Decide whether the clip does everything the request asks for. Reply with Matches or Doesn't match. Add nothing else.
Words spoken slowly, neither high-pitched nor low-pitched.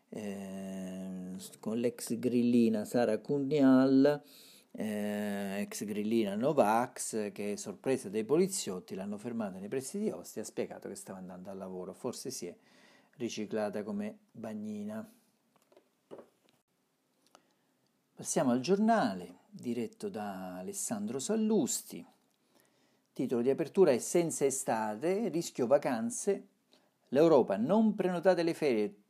Matches